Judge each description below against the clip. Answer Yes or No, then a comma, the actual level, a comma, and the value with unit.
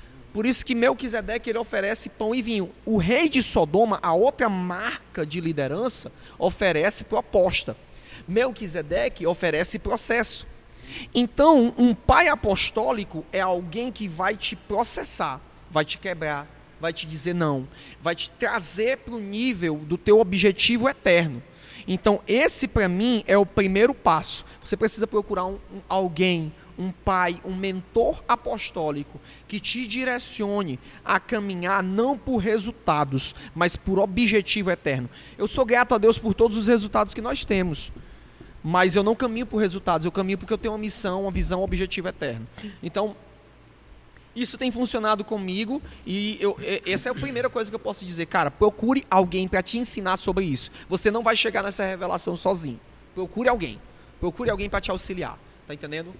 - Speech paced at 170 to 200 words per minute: No, average, 160 wpm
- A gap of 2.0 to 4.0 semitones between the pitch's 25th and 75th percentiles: No, average, 4.5 semitones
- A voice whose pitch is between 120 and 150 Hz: No, high, 200 Hz